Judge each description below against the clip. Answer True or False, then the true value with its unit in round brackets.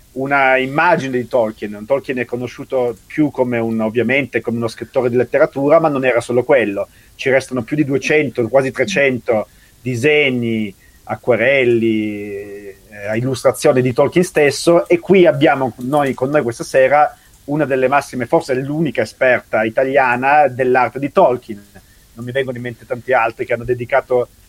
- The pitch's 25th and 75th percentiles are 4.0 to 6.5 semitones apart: False (3.1 semitones)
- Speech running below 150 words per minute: False (155 wpm)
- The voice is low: True (130 Hz)